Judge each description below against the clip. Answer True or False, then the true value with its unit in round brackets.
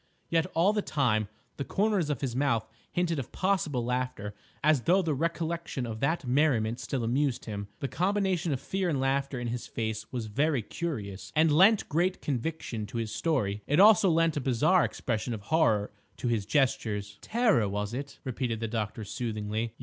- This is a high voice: False (135 Hz)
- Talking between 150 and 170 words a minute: False (180 wpm)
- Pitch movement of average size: False (6.6 semitones)